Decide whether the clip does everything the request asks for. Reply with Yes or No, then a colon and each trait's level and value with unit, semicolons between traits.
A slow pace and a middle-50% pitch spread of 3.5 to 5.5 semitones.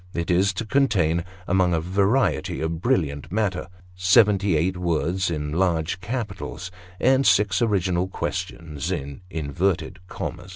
No: slow, 130 wpm; average, 3.0 semitones